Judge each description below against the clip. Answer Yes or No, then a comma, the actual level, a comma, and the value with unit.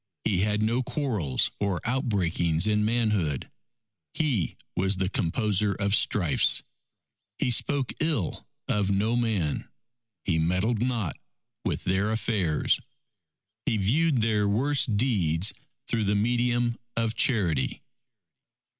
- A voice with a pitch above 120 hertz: No, low, 105 Hz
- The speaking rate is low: Yes, slow, 115 wpm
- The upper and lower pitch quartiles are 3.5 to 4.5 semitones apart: Yes, average, 4.1 semitones